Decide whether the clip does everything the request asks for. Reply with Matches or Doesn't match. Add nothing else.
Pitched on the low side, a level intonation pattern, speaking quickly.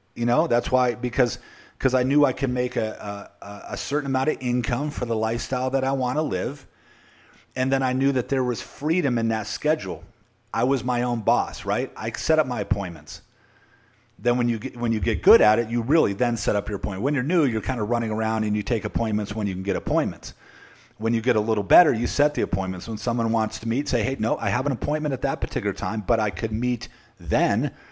Doesn't match